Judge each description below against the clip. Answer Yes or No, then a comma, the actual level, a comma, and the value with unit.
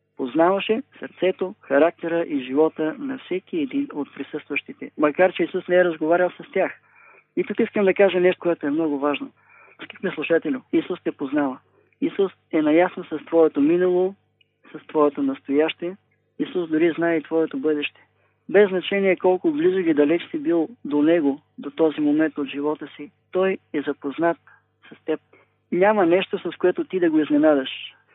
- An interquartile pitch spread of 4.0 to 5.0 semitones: Yes, average, 4.7 semitones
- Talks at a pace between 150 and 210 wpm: Yes, fast, 165 wpm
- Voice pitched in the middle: Yes, medium, 170 Hz